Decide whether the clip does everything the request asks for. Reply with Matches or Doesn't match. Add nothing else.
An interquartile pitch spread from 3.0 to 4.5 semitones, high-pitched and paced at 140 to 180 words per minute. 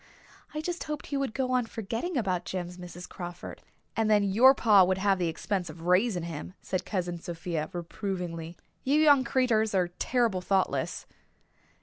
Doesn't match